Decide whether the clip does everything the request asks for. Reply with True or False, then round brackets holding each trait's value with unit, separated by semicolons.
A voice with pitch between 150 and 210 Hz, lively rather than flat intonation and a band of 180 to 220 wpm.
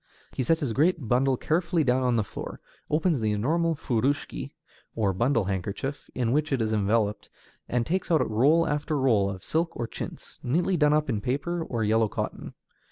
False (130 Hz; 5.8 semitones; 185 wpm)